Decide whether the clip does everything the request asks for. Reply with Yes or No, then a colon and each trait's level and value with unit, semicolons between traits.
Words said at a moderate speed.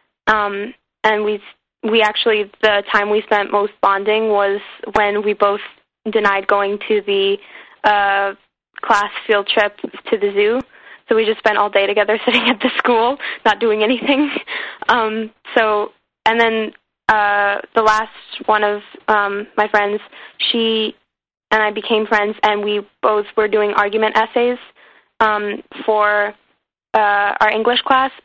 Yes: average, 150 wpm